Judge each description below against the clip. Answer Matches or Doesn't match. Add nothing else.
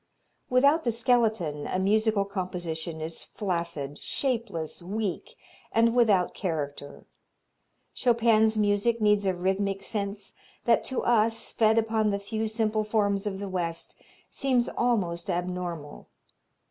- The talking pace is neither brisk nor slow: Doesn't match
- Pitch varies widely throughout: Doesn't match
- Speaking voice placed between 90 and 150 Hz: Doesn't match